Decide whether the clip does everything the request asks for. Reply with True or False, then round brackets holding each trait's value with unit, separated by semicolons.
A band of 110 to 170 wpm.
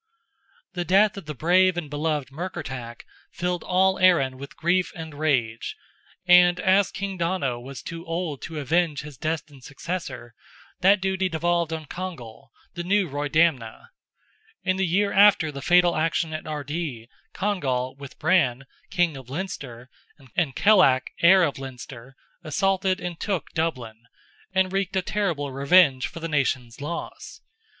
True (145 wpm)